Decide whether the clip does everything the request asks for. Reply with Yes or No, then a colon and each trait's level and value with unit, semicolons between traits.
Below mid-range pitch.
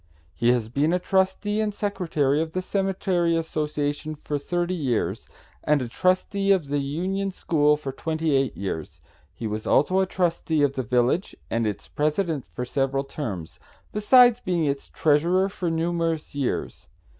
No: medium, 155 Hz